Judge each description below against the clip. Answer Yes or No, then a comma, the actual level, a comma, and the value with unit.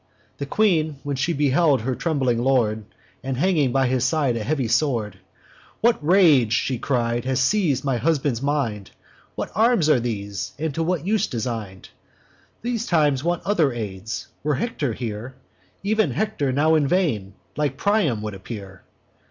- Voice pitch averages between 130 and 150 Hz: Yes, low, 135 Hz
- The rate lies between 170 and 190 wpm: No, average, 160 wpm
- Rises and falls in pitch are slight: No, wide, 5.5 semitones